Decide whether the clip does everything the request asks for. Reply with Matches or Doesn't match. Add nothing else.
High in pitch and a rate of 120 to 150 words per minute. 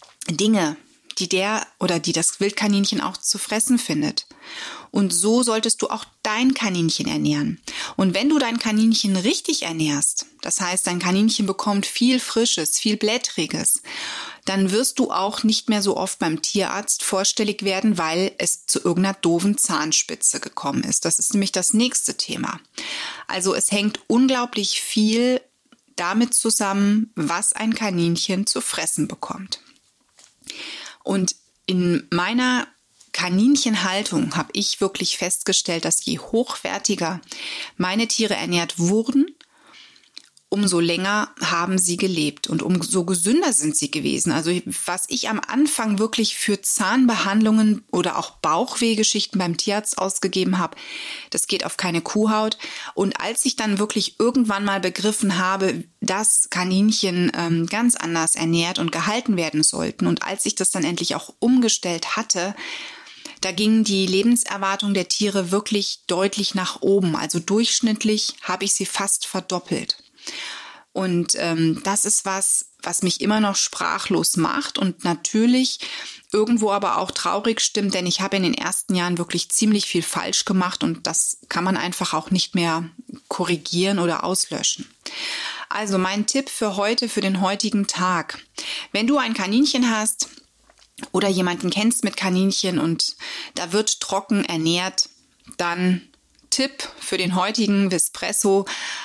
Matches